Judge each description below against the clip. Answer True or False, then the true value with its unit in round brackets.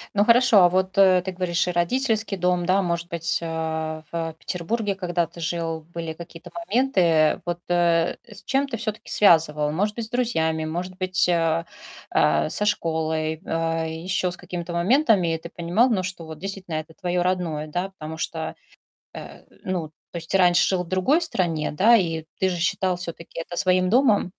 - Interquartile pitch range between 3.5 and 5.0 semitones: False (2.6 semitones)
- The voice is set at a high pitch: False (175 Hz)